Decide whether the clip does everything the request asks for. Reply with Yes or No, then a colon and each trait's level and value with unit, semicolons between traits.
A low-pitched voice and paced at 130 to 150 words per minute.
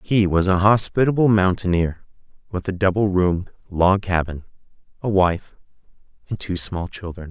Yes: very low, 95 Hz; average, 140 wpm